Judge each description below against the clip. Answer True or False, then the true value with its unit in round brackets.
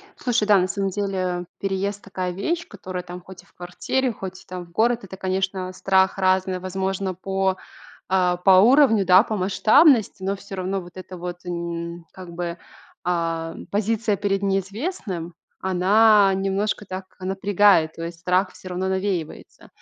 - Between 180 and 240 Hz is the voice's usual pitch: True (190 Hz)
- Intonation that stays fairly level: True (1.9 semitones)